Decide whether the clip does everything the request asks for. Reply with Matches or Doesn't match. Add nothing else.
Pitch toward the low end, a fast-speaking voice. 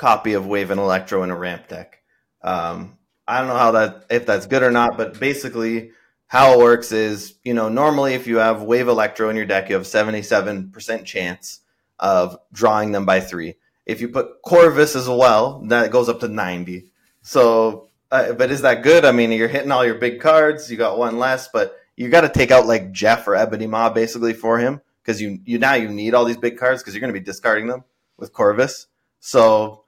Matches